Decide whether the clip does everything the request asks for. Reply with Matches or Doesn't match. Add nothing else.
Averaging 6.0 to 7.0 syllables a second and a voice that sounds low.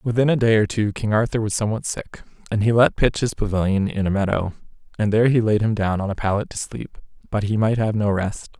Matches